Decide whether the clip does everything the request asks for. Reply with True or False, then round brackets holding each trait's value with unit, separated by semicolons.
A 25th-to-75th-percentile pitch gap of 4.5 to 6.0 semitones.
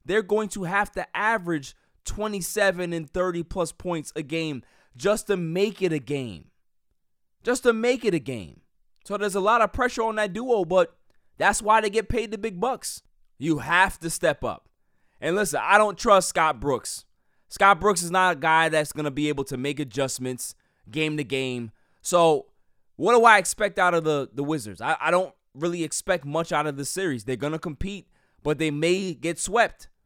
True (5.6 semitones)